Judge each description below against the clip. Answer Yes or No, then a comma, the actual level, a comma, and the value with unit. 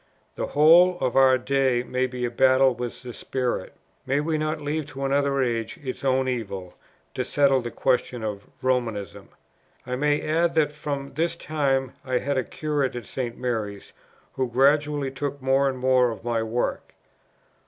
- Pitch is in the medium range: No, low, 130 Hz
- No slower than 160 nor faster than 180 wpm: Yes, average, 175 wpm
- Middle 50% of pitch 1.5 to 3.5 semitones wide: Yes, average, 2.8 semitones